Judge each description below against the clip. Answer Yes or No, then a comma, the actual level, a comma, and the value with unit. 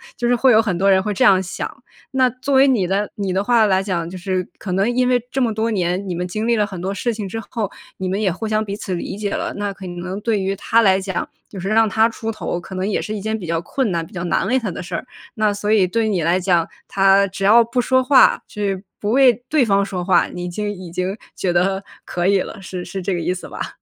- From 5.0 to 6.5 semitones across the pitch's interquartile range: No, average, 3.2 semitones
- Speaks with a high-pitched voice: Yes, high, 200 Hz